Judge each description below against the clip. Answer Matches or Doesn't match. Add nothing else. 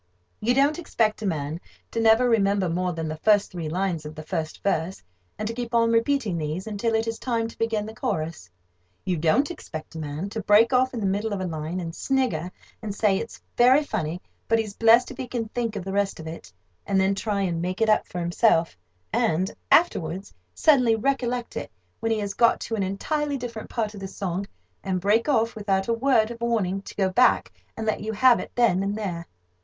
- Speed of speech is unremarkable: Doesn't match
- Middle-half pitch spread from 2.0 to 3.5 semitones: Doesn't match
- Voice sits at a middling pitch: Doesn't match